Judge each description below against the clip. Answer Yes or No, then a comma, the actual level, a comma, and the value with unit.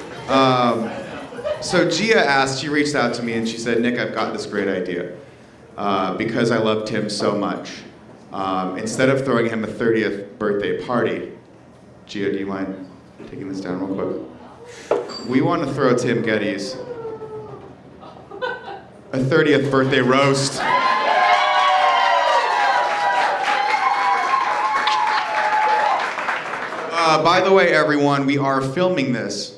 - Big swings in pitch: Yes, wide, 6.4 semitones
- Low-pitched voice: Yes, low, 125 Hz